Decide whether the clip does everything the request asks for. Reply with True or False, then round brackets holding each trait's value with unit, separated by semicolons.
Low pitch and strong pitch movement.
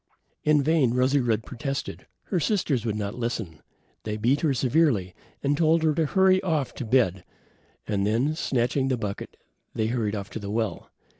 True (125 Hz; 5.8 semitones)